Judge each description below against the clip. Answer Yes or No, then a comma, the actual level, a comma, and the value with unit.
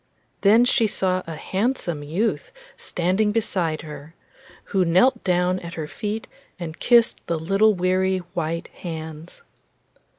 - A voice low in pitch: No, medium, 185 Hz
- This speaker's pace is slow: Yes, slow, 130 wpm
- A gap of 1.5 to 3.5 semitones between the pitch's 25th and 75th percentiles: No, average, 4.1 semitones